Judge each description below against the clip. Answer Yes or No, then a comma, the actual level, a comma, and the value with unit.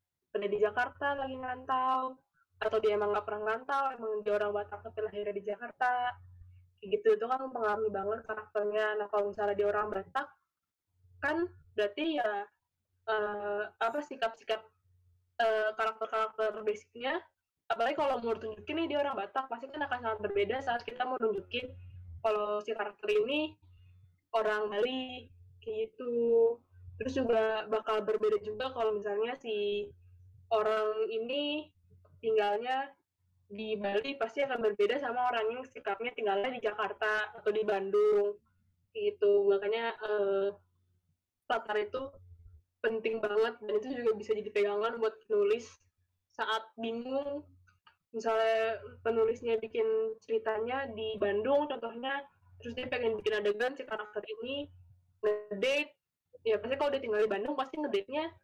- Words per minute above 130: Yes, fast, 140 wpm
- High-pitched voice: Yes, high, 220 Hz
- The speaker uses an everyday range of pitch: Yes, average, 3.9 semitones